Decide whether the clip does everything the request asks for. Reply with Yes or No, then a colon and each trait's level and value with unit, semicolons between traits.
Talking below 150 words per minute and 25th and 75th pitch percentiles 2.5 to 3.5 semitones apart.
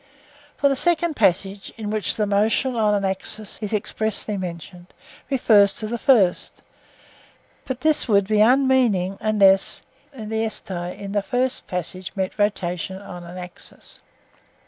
Yes: slow, 135 wpm; average, 3.2 semitones